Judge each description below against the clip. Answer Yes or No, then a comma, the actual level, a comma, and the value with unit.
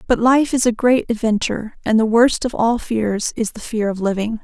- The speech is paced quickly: Yes, fast, 230 wpm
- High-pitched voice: Yes, high, 225 Hz